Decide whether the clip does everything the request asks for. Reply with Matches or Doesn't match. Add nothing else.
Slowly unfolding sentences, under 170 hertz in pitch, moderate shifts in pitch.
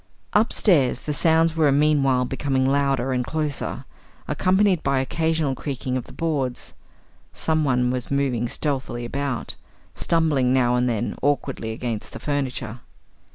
Matches